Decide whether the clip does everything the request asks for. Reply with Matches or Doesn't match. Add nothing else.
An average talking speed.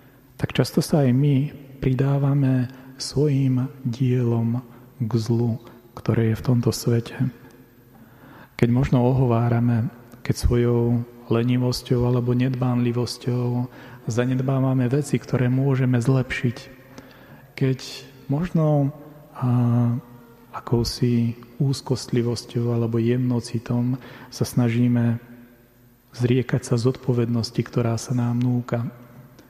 Doesn't match